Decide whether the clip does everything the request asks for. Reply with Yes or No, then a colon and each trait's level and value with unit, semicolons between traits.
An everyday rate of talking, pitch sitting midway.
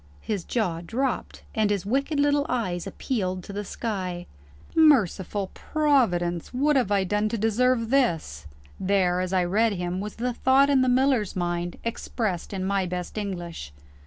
No: average, 160 wpm; high, 205 Hz